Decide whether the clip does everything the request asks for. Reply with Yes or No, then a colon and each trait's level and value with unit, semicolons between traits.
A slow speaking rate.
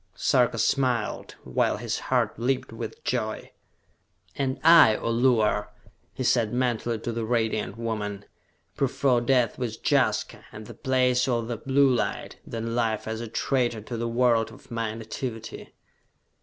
No: average, 150 wpm